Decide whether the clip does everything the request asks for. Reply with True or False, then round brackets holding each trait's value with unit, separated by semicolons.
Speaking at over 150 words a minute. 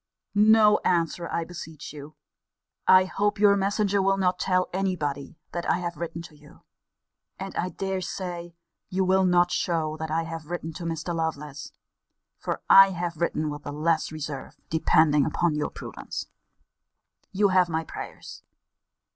True (160 wpm)